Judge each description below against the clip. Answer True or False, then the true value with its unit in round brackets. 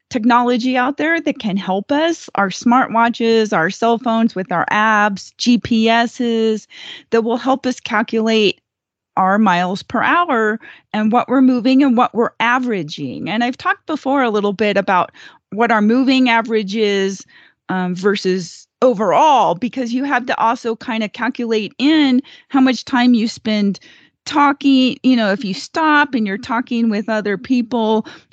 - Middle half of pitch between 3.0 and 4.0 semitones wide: True (3.3 semitones)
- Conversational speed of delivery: True (160 wpm)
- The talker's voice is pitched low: False (230 Hz)